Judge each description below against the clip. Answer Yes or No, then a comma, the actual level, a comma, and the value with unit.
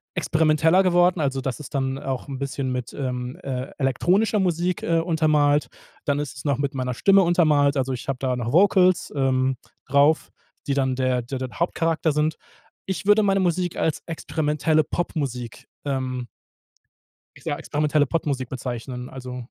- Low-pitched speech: No, medium, 145 Hz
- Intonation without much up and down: No, average, 4.0 semitones